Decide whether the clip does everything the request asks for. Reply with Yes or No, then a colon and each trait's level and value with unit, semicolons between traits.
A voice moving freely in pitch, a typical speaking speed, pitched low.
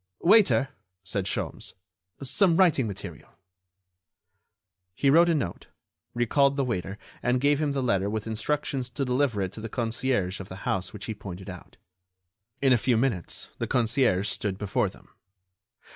Yes: wide, 5.8 semitones; average, 160 wpm; low, 120 Hz